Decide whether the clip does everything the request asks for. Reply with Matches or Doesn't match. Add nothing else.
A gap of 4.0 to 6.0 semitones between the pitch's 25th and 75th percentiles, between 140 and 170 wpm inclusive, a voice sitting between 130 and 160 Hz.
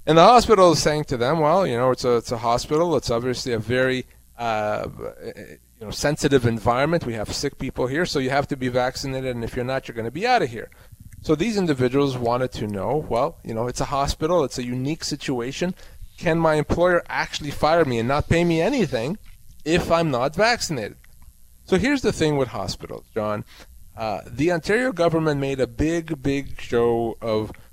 Doesn't match